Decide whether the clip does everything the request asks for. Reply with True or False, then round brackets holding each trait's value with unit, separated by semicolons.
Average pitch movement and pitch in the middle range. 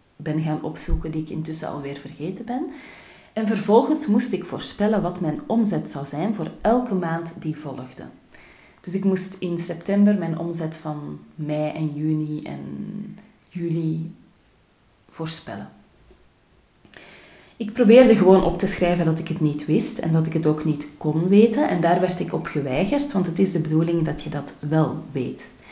True (4.0 semitones; 165 Hz)